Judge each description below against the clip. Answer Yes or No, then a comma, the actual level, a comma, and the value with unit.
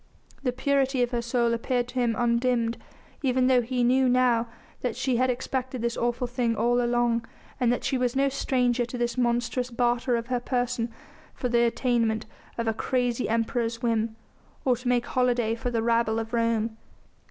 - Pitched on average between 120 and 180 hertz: No, high, 240 Hz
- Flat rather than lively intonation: Yes, narrow, 1.3 semitones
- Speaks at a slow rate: No, average, 185 wpm